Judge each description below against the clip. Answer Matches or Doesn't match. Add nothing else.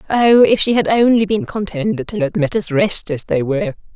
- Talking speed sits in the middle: Doesn't match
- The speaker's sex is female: Matches